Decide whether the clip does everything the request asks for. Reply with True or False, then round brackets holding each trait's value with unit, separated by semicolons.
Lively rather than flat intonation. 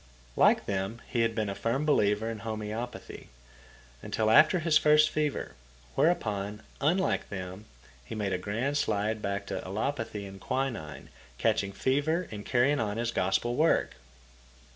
True (5.8 semitones)